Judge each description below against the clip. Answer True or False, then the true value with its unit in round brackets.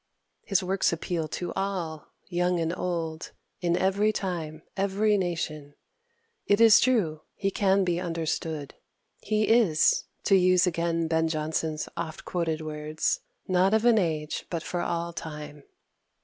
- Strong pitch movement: False (3.4 semitones)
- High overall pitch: False (170 Hz)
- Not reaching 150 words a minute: True (140 wpm)